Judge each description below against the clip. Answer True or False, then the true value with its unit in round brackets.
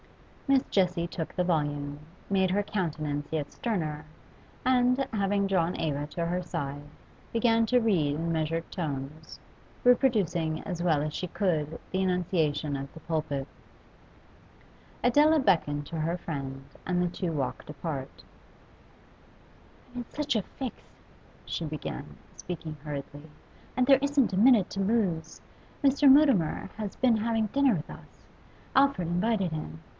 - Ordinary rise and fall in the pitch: False (6.4 semitones)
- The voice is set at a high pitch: False (175 Hz)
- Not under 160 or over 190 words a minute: False (140 wpm)